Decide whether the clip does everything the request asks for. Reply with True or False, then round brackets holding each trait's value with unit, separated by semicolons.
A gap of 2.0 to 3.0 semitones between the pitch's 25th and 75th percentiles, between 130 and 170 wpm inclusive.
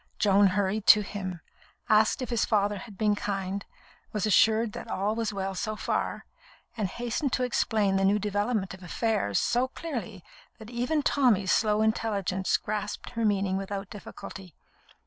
True (2.5 semitones; 160 wpm)